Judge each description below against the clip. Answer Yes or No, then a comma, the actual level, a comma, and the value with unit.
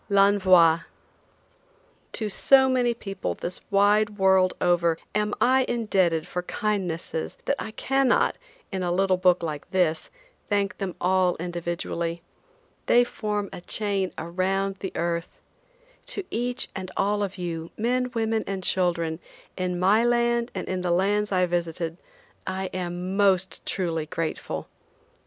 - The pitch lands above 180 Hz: Yes, high, 190 Hz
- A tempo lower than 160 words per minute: Yes, average, 140 wpm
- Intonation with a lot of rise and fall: No, average, 3.1 semitones